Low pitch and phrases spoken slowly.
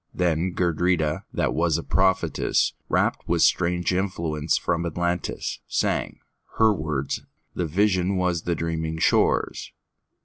Yes: very low, 85 Hz; slow, 110 wpm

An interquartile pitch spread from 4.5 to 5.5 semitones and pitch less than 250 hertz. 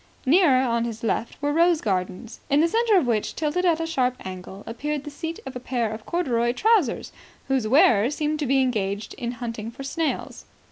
No: average, 5.1 semitones; very high, 260 Hz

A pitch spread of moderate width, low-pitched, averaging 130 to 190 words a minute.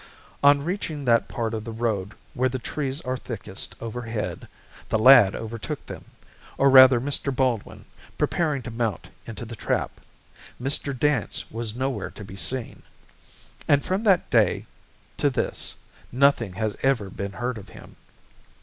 Yes: average, 3.7 semitones; low, 120 Hz; average, 150 wpm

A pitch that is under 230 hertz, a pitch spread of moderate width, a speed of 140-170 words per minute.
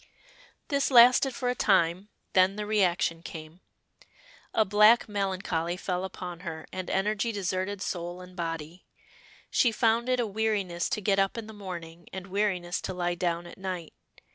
Yes: high, 190 Hz; average, 3.3 semitones; average, 165 wpm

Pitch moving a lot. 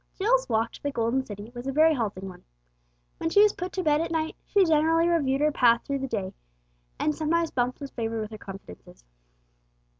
Yes: wide, 6.2 semitones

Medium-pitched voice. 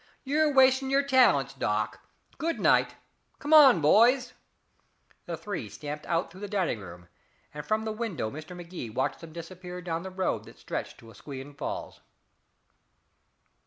Yes: medium, 180 Hz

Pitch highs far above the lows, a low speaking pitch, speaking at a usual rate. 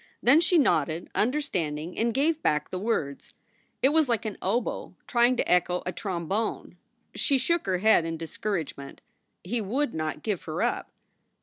No: wide, 7.2 semitones; high, 205 Hz; average, 170 wpm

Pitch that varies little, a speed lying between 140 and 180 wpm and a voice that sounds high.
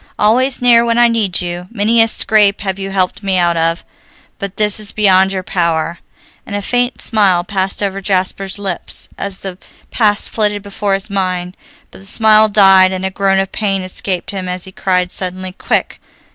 No: narrow, 2.1 semitones; average, 190 wpm; high, 195 Hz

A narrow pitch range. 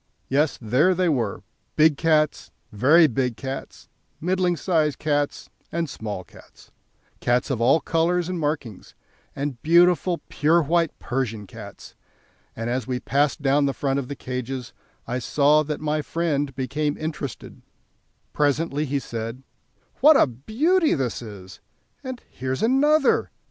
No: average, 4.4 semitones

